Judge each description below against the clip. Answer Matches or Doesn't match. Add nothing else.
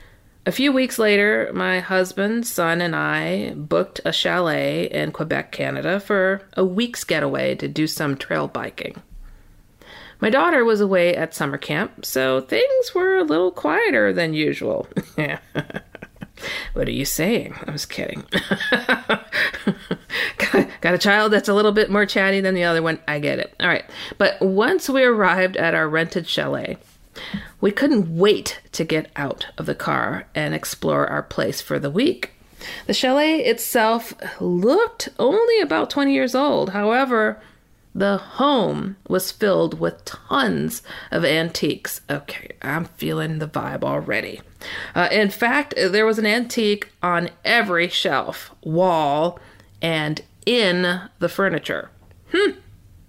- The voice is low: Doesn't match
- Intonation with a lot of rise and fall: Matches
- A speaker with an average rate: Matches